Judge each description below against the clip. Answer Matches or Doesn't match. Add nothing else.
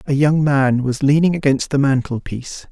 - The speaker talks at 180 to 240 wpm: Matches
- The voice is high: Doesn't match